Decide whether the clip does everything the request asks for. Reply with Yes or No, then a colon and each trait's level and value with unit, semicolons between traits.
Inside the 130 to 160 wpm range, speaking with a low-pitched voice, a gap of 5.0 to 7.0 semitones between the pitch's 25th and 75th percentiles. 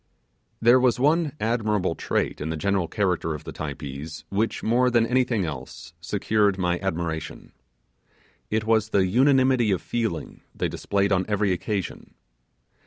Yes: average, 145 wpm; low, 100 Hz; average, 5.3 semitones